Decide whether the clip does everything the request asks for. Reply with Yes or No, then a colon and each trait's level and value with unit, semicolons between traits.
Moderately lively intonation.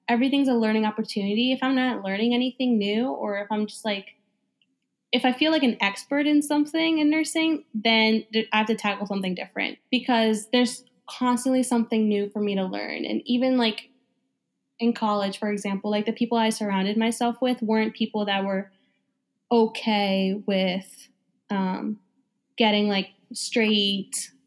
Yes: average, 3.3 semitones